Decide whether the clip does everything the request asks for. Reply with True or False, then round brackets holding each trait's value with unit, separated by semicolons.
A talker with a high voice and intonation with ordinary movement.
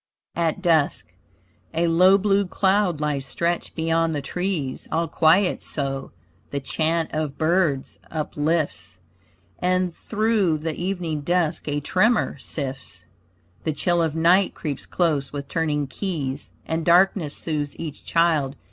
False (160 Hz; 3.4 semitones)